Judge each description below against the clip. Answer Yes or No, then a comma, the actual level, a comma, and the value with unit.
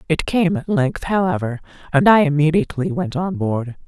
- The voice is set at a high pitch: No, medium, 165 Hz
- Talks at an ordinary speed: Yes, average, 170 wpm